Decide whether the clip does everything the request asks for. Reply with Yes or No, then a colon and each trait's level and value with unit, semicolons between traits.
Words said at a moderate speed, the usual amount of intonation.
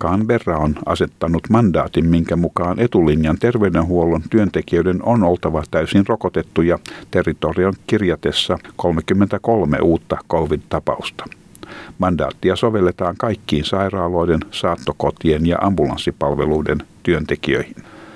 No: slow, 85 wpm; average, 3.6 semitones